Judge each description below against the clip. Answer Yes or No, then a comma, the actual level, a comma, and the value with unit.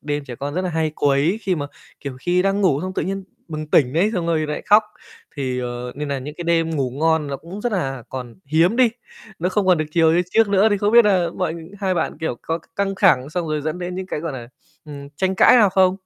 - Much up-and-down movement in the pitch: No, average, 4.6 semitones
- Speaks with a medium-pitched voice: Yes, medium, 165 Hz